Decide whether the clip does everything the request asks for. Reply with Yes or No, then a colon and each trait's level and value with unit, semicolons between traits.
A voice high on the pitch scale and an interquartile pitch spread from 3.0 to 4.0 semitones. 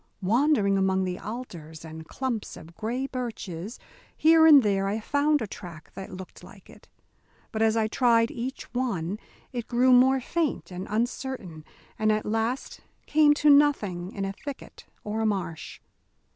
No: high, 220 Hz; average, 5.3 semitones